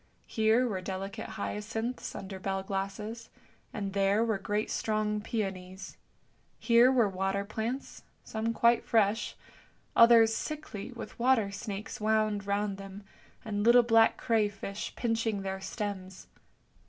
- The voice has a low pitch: No, high, 210 Hz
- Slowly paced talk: Yes, slow, 130 wpm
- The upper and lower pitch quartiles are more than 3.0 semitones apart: No, narrow, 2.5 semitones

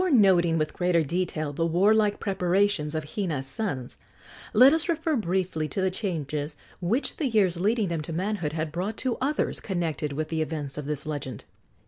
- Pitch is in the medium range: Yes, medium, 175 Hz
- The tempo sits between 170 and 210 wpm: Yes, average, 180 wpm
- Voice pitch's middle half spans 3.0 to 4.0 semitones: No, average, 5.1 semitones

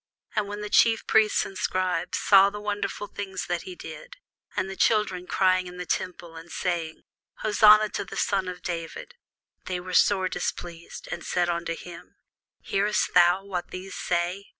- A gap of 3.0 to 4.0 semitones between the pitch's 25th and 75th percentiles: No, narrow, 2.6 semitones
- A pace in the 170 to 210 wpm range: Yes, average, 175 wpm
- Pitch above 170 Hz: Yes, medium, 185 Hz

